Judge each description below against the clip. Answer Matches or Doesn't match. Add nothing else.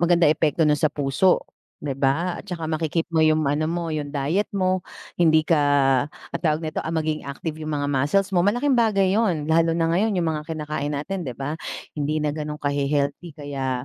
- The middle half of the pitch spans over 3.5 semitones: Doesn't match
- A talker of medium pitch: Matches